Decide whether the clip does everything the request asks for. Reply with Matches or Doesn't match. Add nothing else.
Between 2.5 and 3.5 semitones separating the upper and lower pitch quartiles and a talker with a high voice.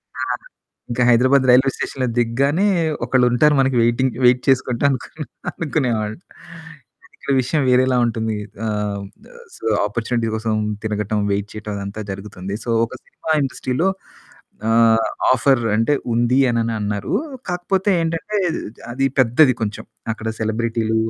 Doesn't match